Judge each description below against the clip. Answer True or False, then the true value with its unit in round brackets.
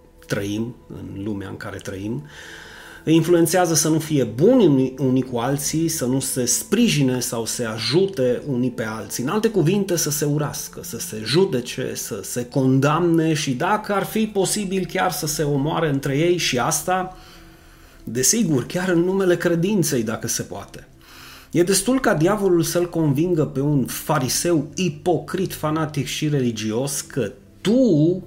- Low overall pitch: False (150 Hz)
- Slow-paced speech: False (155 wpm)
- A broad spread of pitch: True (6.0 semitones)